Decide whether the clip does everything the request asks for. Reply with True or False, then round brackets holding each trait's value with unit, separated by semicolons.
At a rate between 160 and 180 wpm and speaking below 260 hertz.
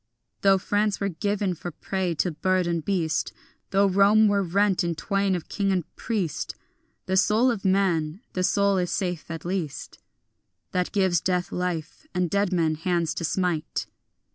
True (165 wpm; 185 Hz)